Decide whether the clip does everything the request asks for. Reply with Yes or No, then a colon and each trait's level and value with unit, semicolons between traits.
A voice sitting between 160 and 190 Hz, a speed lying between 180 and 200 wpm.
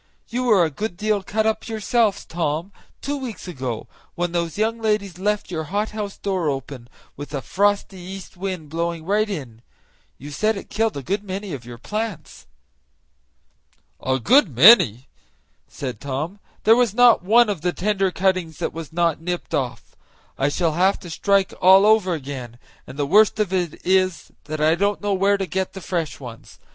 Yes: medium, 185 Hz; average, 185 wpm